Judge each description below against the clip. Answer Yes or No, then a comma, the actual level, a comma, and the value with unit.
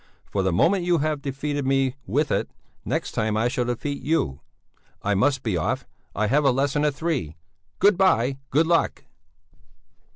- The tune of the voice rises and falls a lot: No, average, 4.8 semitones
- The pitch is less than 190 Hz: Yes, low, 135 Hz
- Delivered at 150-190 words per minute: Yes, average, 170 wpm